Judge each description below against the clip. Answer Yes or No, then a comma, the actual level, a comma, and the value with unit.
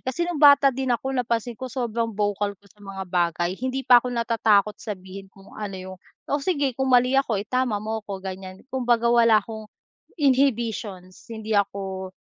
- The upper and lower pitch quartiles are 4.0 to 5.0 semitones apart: Yes, average, 4.4 semitones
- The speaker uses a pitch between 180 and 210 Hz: No, high, 220 Hz